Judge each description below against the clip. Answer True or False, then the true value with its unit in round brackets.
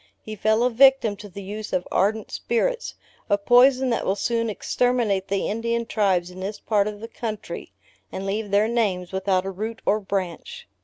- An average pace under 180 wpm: False (190 wpm)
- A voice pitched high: True (215 Hz)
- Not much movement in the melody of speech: False (3.1 semitones)